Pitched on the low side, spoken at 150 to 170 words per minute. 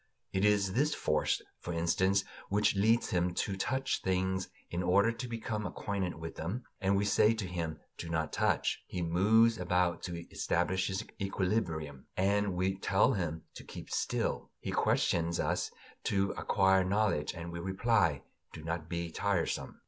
Yes: very low, 95 Hz; average, 165 wpm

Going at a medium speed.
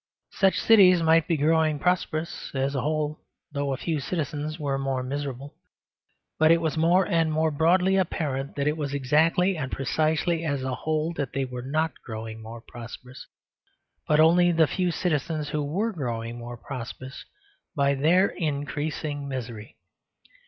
Yes: average, 160 wpm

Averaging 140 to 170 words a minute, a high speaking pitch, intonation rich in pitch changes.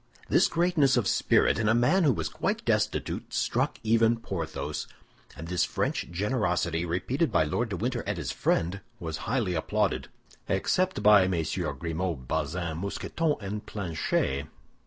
No: average, 150 wpm; very low, 95 Hz; wide, 5.8 semitones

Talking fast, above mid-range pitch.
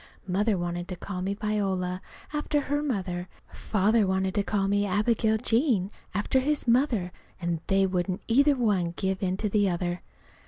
No: average, 170 wpm; high, 200 Hz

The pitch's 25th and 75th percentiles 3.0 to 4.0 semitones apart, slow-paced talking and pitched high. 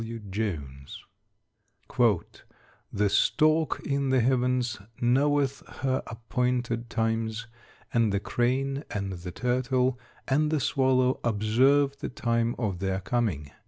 No: average, 3.4 semitones; slow, 120 wpm; low, 120 Hz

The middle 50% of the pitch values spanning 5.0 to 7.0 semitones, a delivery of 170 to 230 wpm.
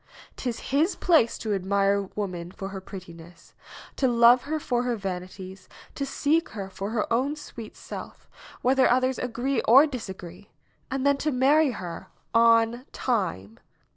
No: wide, 5.4 semitones; average, 160 wpm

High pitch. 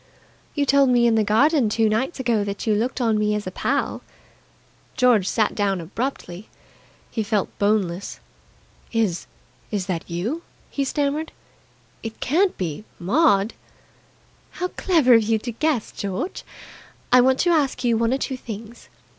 Yes: high, 225 Hz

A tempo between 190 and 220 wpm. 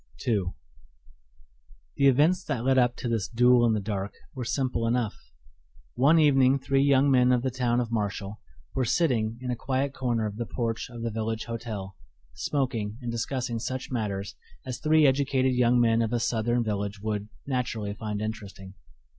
No: average, 175 wpm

